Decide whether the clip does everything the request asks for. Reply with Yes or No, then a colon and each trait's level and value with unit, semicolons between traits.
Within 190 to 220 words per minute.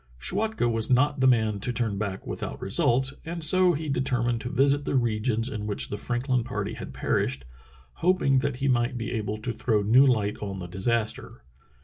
Yes: average, 195 wpm